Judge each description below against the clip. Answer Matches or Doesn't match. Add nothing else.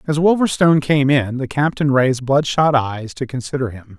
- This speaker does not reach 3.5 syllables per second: Doesn't match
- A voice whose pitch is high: Doesn't match